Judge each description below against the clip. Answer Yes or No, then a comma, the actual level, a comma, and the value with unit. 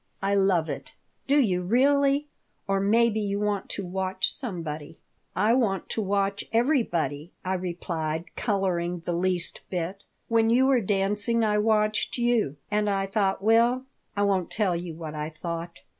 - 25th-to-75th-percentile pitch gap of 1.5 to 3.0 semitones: No, average, 4.1 semitones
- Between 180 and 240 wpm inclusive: No, average, 160 wpm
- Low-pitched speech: No, high, 195 Hz